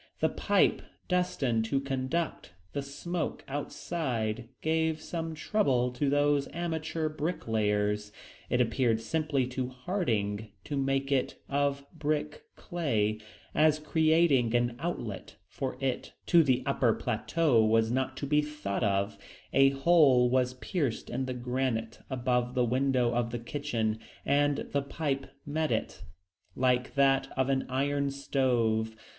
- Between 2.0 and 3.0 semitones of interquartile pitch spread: No, average, 3.6 semitones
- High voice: No, low, 135 Hz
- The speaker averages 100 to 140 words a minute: Yes, slow, 135 wpm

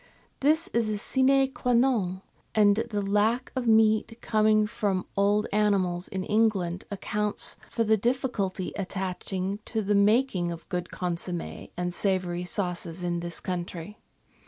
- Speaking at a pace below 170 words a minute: Yes, average, 145 wpm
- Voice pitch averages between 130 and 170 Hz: No, high, 205 Hz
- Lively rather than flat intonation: No, average, 3.4 semitones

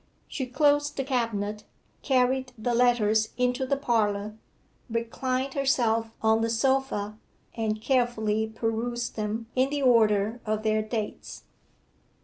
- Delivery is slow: Yes, slow, 125 wpm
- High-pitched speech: Yes, high, 230 Hz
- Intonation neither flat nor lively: Yes, average, 3.0 semitones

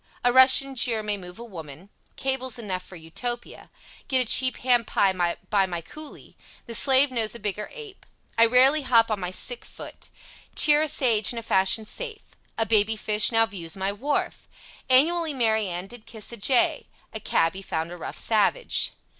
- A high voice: Yes, high, 225 Hz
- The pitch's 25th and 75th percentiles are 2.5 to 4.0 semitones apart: No, average, 4.9 semitones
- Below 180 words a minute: No, average, 185 wpm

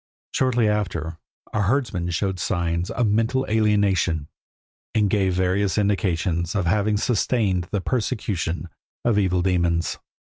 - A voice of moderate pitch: No, very low, 95 Hz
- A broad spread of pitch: No, average, 3.3 semitones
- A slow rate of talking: Yes, slow, 120 wpm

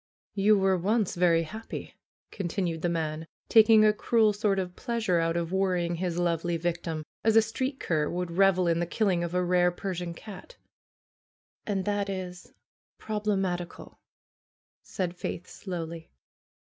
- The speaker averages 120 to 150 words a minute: Yes, average, 145 wpm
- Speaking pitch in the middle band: Yes, medium, 180 Hz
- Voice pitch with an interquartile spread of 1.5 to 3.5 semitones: Yes, average, 3.2 semitones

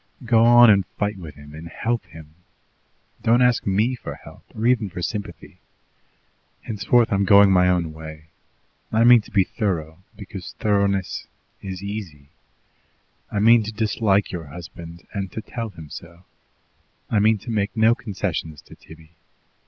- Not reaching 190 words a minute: Yes, average, 160 wpm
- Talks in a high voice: No, low, 100 Hz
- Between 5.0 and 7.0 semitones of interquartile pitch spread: No, average, 4.6 semitones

